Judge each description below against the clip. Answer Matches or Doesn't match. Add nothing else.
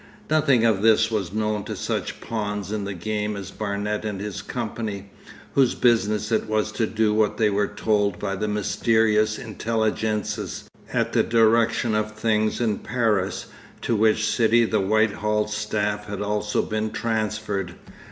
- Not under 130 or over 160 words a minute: Matches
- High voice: Doesn't match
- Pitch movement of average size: Doesn't match